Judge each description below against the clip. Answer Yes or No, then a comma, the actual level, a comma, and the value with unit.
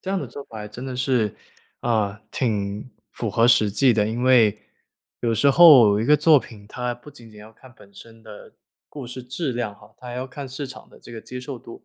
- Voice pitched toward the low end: Yes, low, 120 Hz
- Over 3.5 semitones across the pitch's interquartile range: No, average, 3.2 semitones